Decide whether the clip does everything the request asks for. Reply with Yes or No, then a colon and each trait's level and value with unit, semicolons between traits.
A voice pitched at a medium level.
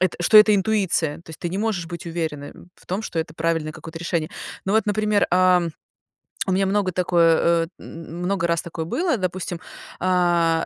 Yes: medium, 175 Hz